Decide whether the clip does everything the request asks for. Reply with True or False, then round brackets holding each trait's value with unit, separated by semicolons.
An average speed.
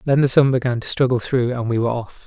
False (290 wpm)